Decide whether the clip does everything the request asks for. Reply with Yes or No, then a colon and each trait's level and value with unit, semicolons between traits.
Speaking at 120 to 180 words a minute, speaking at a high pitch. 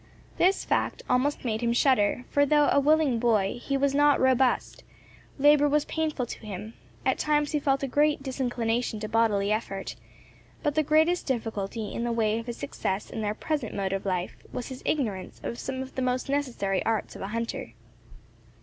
No: average, 190 wpm; very high, 250 Hz